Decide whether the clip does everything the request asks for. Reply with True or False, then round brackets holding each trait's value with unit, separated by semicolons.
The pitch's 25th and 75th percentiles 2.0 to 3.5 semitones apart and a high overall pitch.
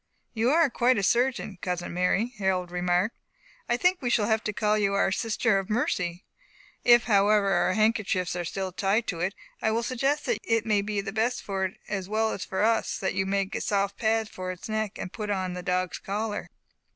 True (2.9 semitones; 205 Hz)